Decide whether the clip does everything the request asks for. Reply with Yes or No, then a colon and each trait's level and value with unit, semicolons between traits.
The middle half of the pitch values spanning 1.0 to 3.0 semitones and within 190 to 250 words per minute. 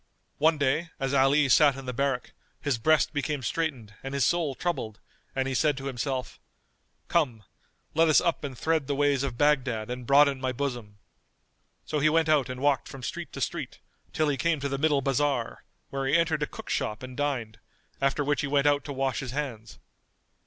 Yes: narrow, 2.4 semitones; average, 200 wpm